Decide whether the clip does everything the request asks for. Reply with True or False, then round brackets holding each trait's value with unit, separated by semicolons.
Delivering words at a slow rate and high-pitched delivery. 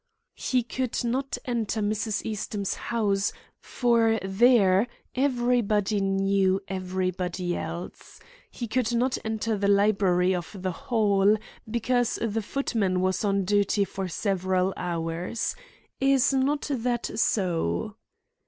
True (115 wpm; 205 Hz)